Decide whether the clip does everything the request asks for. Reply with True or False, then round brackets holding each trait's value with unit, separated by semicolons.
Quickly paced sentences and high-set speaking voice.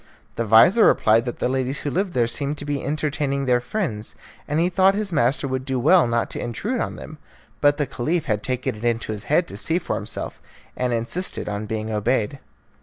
False (215 wpm; 130 Hz)